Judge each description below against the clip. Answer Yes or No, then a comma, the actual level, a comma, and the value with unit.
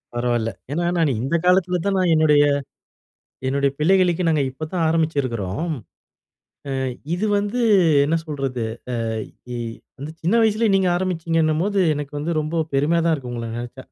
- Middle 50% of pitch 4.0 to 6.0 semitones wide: Yes, average, 4.4 semitones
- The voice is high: No, medium, 160 Hz